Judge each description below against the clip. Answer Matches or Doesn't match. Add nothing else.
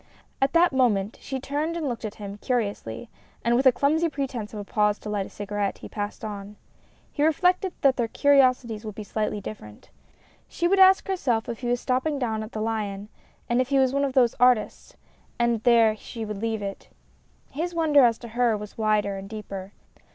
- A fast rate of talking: Matches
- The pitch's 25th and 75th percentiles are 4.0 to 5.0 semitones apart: Matches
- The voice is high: Matches